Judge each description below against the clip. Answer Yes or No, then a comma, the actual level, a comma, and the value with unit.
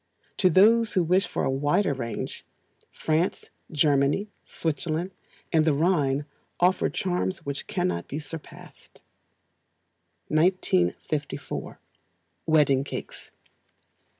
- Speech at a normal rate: No, slow, 95 wpm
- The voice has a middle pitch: Yes, medium, 155 Hz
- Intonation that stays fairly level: No, average, 4.4 semitones